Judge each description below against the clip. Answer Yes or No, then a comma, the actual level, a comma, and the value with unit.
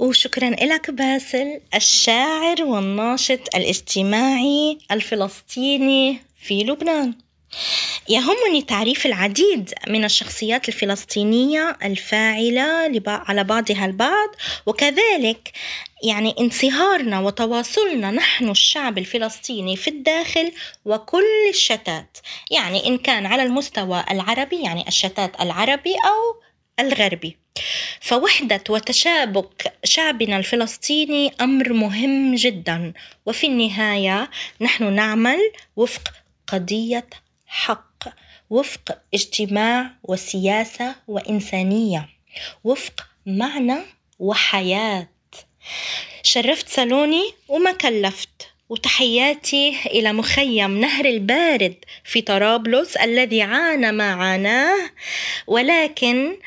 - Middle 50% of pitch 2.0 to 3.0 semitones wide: No, average, 5.1 semitones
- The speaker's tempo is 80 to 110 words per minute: Yes, average, 85 wpm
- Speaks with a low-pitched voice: No, high, 240 Hz